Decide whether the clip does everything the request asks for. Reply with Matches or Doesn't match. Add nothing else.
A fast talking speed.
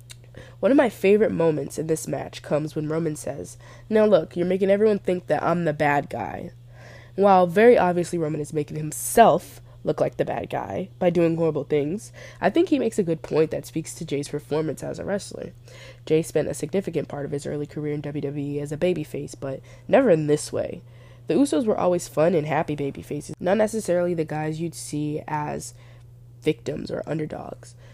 Doesn't match